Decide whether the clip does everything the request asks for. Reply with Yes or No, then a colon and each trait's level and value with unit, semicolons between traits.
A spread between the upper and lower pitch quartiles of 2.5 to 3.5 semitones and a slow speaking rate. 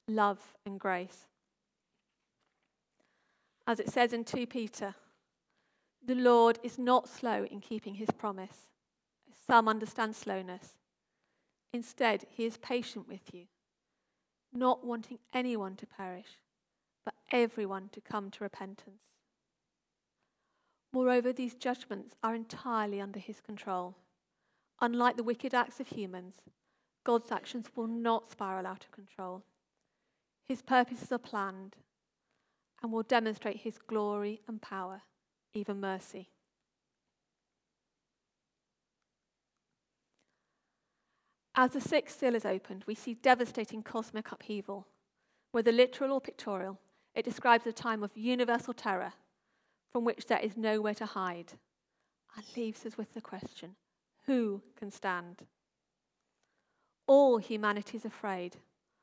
Yes: average, 3.2 semitones; slow, 115 wpm